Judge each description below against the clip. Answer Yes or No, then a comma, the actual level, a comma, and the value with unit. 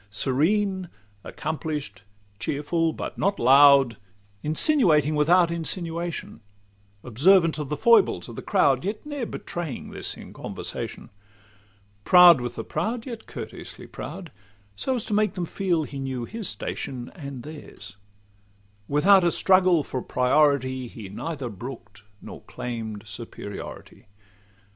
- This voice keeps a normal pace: No, slow, 125 wpm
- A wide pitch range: Yes, wide, 6.6 semitones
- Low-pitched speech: No, medium, 150 Hz